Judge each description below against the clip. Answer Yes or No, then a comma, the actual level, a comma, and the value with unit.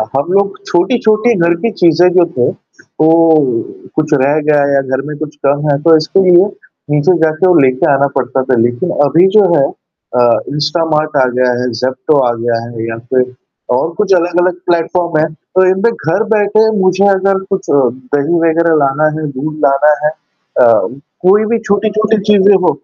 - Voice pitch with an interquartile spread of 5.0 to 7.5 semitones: Yes, average, 5.3 semitones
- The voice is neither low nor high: Yes, medium, 155 Hz